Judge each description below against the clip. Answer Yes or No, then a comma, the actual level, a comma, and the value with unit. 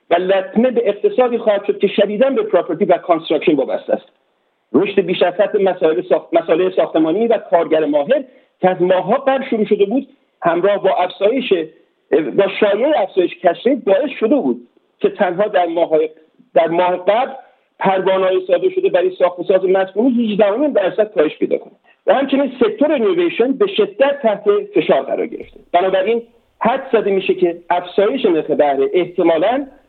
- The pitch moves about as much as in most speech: No, wide, 5.9 semitones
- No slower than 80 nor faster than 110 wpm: No, fast, 155 wpm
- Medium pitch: No, high, 200 Hz